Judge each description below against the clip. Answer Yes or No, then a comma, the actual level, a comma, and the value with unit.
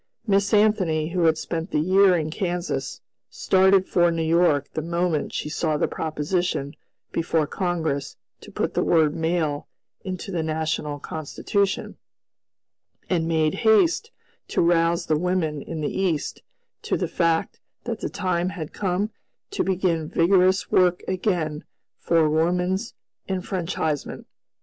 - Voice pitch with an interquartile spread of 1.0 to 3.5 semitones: Yes, average, 2.9 semitones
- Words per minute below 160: Yes, slow, 135 wpm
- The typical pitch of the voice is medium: Yes, medium, 170 Hz